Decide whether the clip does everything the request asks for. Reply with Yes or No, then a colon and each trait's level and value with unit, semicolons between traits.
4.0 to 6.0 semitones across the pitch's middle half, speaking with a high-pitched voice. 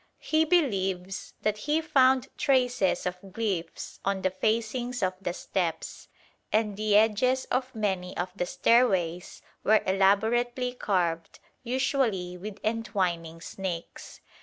Yes: average, 5.0 semitones; high, 210 Hz